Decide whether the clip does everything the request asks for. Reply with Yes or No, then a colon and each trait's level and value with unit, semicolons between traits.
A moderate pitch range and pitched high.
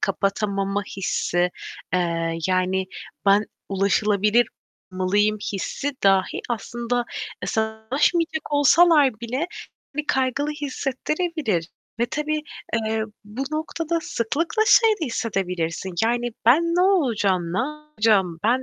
No: wide, 7.3 semitones; high, 230 Hz